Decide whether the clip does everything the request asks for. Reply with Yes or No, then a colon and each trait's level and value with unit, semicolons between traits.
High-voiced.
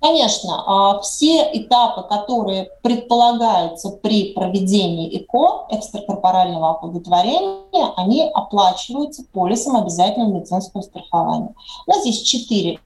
Yes: high, 210 Hz